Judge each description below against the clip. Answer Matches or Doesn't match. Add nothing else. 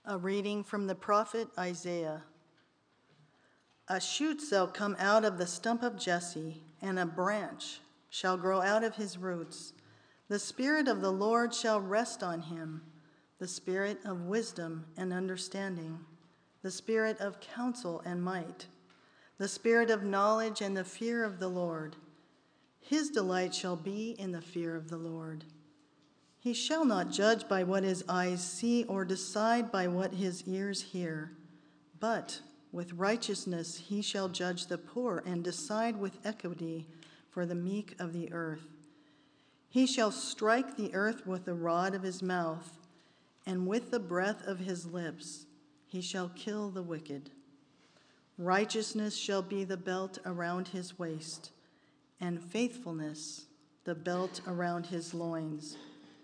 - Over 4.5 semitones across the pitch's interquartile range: Doesn't match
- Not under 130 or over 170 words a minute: Matches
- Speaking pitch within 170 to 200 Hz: Matches